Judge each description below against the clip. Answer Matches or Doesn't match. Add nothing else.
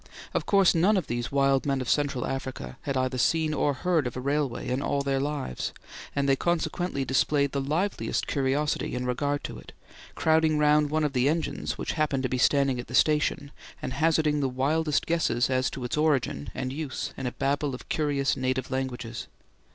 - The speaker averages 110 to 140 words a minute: Doesn't match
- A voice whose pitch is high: Doesn't match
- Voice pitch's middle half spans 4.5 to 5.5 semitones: Doesn't match